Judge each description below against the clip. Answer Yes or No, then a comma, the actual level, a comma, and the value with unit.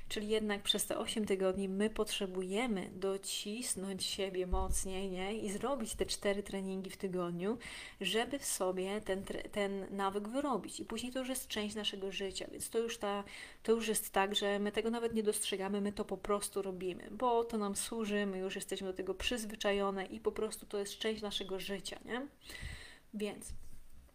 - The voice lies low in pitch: No, high, 205 Hz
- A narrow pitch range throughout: Yes, narrow, 2.0 semitones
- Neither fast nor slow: No, fast, 180 wpm